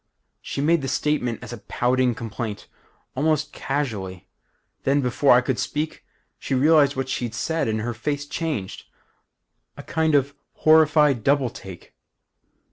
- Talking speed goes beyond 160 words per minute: No, average, 140 wpm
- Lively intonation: No, average, 4.0 semitones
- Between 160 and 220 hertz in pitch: No, low, 135 Hz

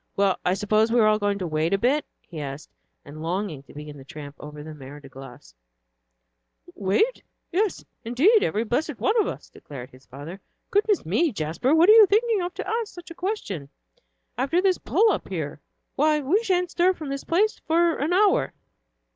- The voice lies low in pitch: No, high, 230 Hz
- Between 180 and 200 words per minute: Yes, average, 195 wpm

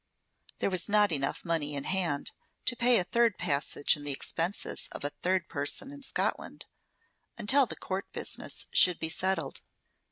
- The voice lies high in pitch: No, medium, 180 Hz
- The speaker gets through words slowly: No, average, 165 wpm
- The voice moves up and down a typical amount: No, wide, 6.2 semitones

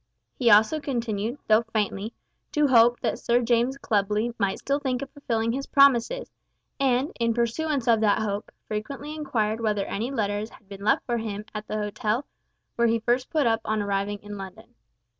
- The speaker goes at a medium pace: Yes, average, 180 wpm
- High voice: Yes, high, 230 Hz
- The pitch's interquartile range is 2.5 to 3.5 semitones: Yes, average, 3.2 semitones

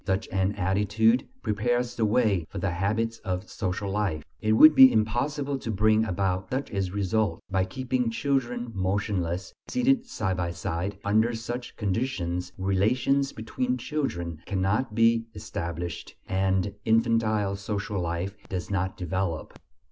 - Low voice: Yes, low, 105 Hz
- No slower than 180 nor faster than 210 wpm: No, average, 140 wpm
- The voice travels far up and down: No, average, 3.6 semitones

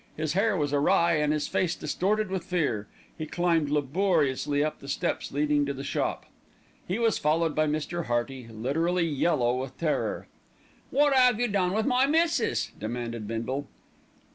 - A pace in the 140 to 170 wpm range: Yes, average, 165 wpm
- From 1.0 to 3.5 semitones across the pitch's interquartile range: No, average, 5.2 semitones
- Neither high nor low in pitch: Yes, medium, 155 Hz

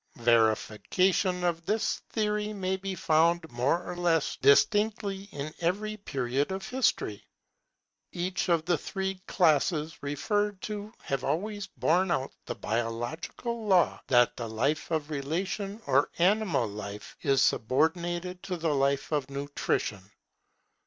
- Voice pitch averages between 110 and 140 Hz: No, medium, 170 Hz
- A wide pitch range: Yes, wide, 5.9 semitones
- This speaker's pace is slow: Yes, slow, 130 wpm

